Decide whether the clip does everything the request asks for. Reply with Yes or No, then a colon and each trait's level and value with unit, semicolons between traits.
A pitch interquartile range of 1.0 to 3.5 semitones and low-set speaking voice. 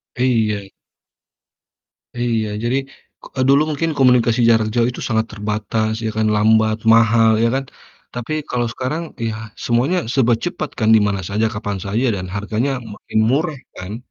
Yes: average, 2.8 semitones; low, 115 Hz